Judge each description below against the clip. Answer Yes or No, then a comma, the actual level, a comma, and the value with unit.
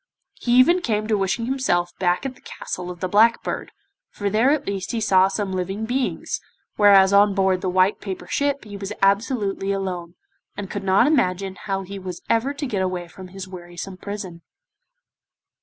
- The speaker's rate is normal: Yes, average, 190 wpm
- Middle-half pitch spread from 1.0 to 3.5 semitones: Yes, average, 3.0 semitones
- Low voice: No, high, 195 Hz